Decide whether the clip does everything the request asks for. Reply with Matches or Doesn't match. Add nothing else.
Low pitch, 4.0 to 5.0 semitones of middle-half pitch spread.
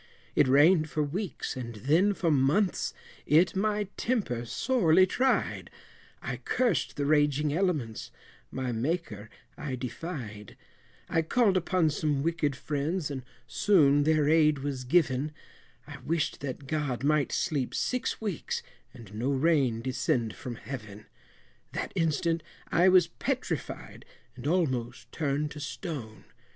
Doesn't match